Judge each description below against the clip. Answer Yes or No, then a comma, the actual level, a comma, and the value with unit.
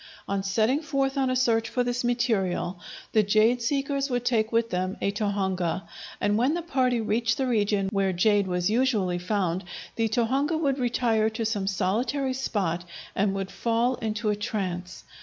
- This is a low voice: No, high, 220 Hz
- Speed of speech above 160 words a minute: Yes, average, 175 wpm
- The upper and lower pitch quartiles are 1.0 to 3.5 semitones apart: No, average, 4.1 semitones